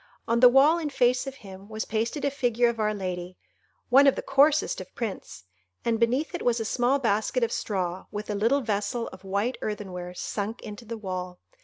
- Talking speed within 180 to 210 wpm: Yes, average, 195 wpm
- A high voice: Yes, high, 225 Hz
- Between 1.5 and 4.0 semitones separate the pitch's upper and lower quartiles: No, average, 4.4 semitones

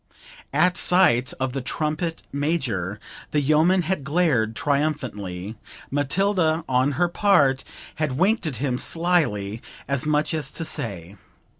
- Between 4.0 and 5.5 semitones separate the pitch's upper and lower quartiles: Yes, average, 5.0 semitones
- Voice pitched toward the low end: No, medium, 145 Hz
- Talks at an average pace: No, slow, 130 wpm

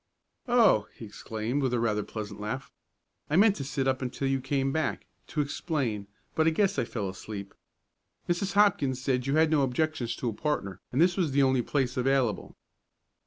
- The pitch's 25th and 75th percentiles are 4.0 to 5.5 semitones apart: Yes, average, 5.1 semitones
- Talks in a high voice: No, low, 135 Hz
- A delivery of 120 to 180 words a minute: No, average, 190 wpm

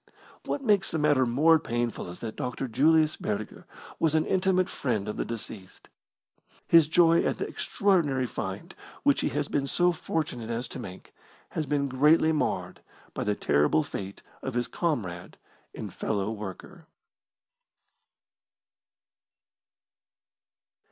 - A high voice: No, low, 135 Hz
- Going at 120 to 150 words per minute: Yes, slow, 135 wpm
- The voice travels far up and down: Yes, wide, 6.7 semitones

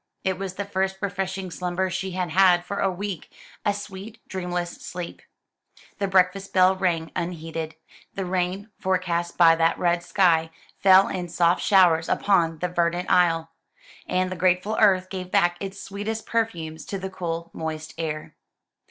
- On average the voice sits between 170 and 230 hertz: Yes, medium, 185 Hz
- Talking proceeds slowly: No, average, 160 wpm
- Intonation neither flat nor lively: No, narrow, 1.9 semitones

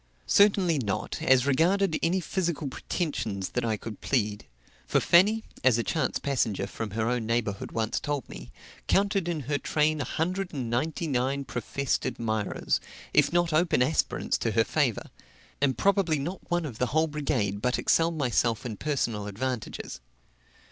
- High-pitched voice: No, medium, 140 Hz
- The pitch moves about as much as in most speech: No, wide, 6.2 semitones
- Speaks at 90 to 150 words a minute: No, average, 160 wpm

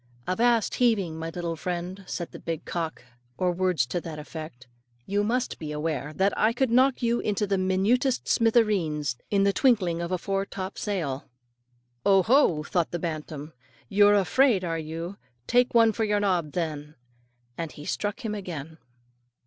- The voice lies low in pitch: No, medium, 185 Hz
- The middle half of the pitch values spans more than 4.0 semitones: Yes, average, 4.6 semitones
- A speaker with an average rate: Yes, average, 165 wpm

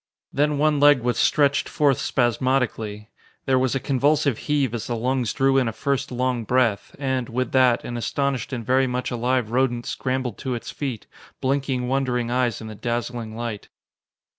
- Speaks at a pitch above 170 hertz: No, low, 130 Hz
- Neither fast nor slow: Yes, average, 175 wpm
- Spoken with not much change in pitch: Yes, narrow, 2.2 semitones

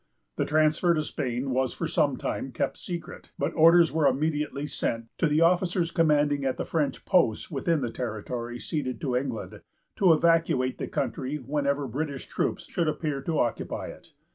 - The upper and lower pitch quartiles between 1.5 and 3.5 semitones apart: No, average, 4.0 semitones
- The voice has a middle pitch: Yes, medium, 145 Hz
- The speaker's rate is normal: Yes, average, 170 wpm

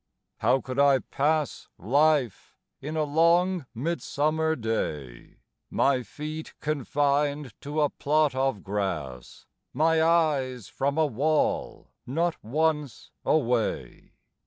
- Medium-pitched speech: Yes, medium, 145 Hz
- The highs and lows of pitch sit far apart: No, average, 3.7 semitones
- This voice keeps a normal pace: No, slow, 110 wpm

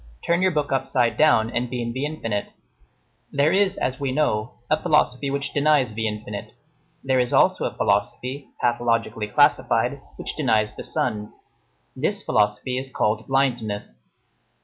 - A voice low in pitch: Yes, low, 125 Hz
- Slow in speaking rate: No, average, 150 wpm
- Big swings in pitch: No, average, 4.3 semitones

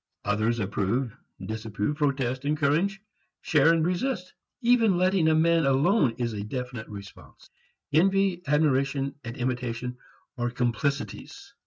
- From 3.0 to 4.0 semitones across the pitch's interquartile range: No, wide, 5.6 semitones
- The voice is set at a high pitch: No, low, 135 Hz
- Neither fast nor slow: No, slow, 120 wpm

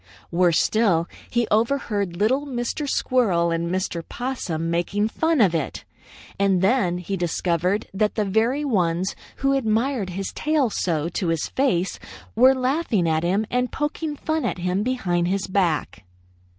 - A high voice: Yes, high, 200 Hz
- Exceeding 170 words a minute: No, average, 150 wpm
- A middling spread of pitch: No, wide, 6.4 semitones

